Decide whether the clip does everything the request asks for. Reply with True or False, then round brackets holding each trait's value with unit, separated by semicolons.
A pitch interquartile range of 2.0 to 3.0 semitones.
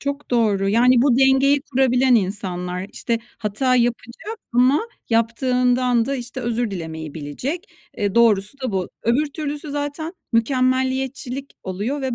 False (3.8 semitones)